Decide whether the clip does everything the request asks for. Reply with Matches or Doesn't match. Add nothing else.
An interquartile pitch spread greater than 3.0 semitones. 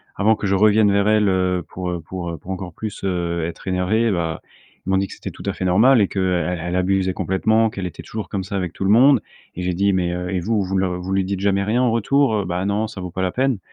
Doesn't match